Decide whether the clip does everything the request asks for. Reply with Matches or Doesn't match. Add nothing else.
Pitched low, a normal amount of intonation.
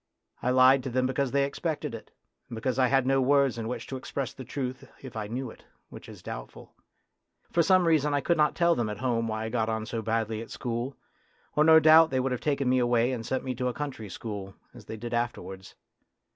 Matches